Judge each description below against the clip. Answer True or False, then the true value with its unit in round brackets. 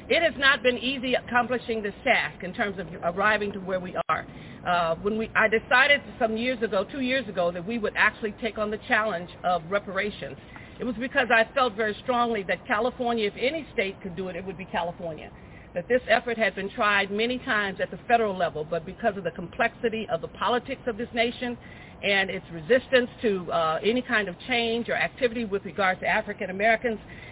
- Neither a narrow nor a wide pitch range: True (4.4 semitones)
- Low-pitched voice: False (215 Hz)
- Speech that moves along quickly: True (210 wpm)